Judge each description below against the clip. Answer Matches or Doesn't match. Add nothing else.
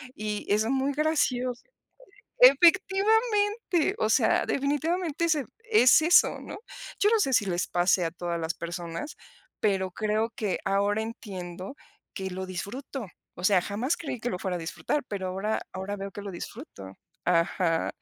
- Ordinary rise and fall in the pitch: Doesn't match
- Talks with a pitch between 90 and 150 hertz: Doesn't match